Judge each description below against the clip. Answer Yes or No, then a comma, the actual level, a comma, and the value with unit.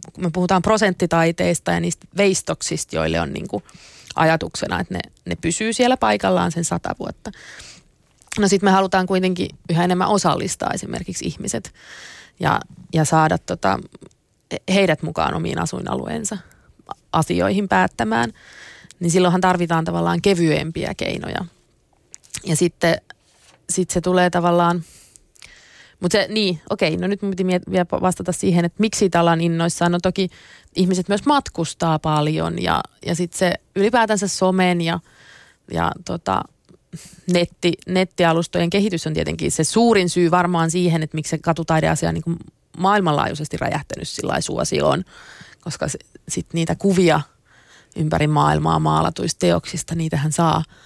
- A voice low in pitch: No, medium, 175 Hz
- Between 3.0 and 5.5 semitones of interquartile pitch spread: No, narrow, 2.4 semitones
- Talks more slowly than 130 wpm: No, average, 135 wpm